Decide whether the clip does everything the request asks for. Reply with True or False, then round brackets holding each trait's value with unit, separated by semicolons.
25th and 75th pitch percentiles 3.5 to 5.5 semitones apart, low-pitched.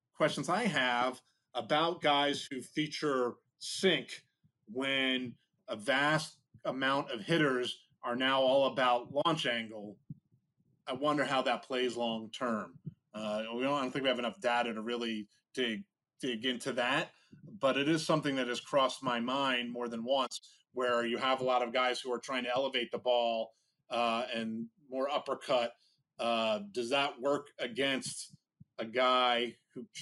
False (2.8 semitones; 125 Hz)